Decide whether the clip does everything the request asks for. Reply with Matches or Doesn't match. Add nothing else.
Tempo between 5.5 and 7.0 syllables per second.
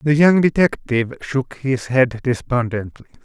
Doesn't match